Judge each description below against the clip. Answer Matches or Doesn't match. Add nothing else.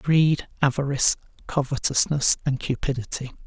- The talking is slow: Matches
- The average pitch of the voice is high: Doesn't match